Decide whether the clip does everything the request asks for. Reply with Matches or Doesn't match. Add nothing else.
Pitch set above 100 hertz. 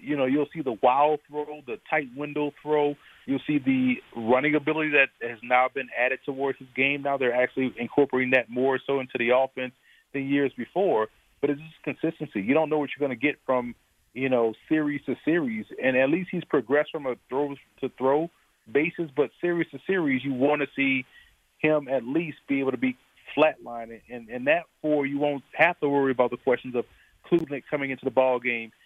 Matches